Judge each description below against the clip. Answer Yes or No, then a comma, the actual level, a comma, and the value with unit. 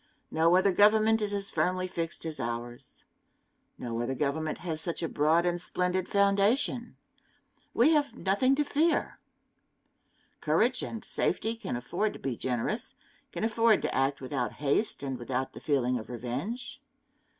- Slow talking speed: No, average, 150 wpm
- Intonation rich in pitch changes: Yes, wide, 8.1 semitones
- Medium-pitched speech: Yes, medium, 175 Hz